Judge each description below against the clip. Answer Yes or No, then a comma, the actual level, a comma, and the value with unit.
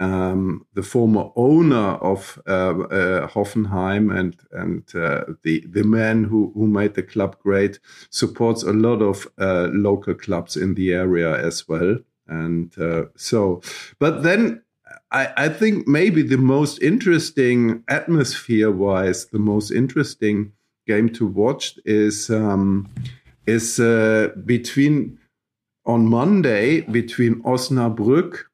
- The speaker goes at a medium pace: No, slow, 130 wpm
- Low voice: Yes, low, 110 Hz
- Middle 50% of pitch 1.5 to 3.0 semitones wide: No, average, 3.7 semitones